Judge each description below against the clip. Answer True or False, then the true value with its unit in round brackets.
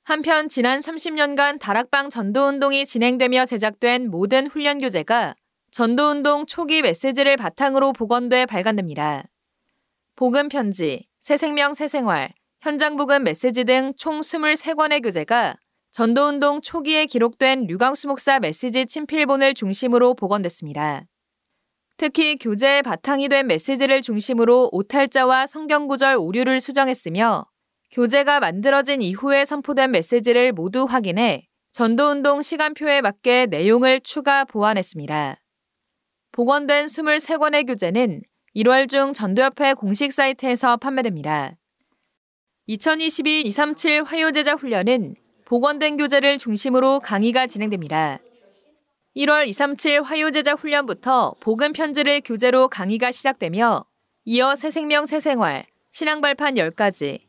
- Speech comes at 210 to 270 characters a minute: False (285 characters per minute)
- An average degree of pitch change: True (3.4 semitones)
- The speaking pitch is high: True (270 Hz)